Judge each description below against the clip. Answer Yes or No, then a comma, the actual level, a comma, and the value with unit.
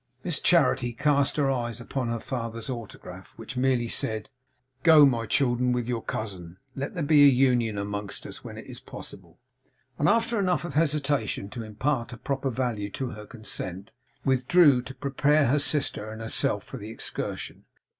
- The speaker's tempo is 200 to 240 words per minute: No, average, 170 wpm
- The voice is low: Yes, low, 125 Hz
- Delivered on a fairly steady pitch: No, average, 4.1 semitones